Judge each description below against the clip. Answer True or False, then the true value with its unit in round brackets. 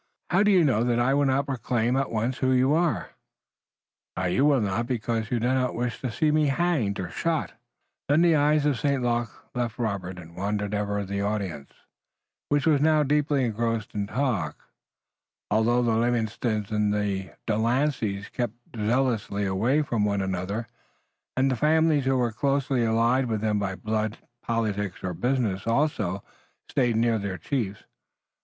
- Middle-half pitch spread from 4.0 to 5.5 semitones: True (4.5 semitones)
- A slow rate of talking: False (170 wpm)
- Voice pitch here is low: True (115 Hz)